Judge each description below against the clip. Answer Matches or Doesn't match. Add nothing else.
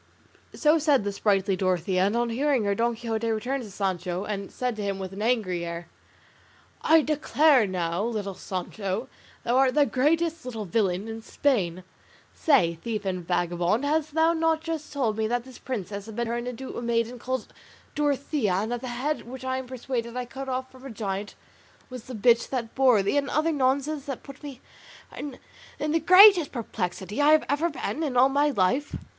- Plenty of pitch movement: Matches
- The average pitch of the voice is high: Matches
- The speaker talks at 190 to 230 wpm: Matches